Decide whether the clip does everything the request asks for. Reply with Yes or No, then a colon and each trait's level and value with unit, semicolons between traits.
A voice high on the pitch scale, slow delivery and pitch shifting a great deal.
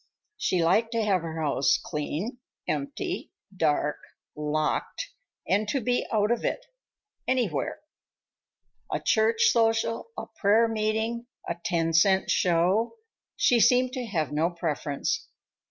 Yes: high, 210 Hz; slow, 120 wpm; wide, 6.1 semitones